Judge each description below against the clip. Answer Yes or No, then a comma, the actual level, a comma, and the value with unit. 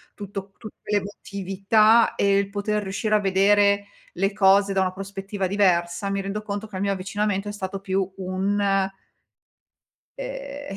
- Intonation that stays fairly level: Yes, narrow, 1.2 semitones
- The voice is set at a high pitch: Yes, high, 200 Hz